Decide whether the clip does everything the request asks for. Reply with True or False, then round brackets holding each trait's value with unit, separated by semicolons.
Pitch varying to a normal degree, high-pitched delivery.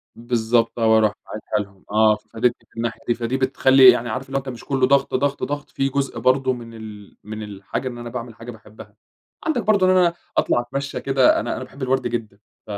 False (3.3 semitones; 120 Hz)